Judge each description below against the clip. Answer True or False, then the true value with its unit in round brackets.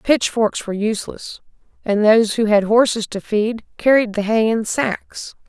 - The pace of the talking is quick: False (165 wpm)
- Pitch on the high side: True (220 Hz)